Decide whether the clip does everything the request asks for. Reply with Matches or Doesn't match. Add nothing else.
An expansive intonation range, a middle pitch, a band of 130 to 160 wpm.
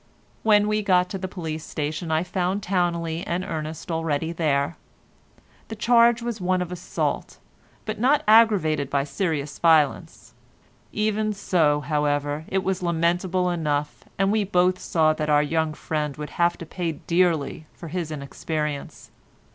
Doesn't match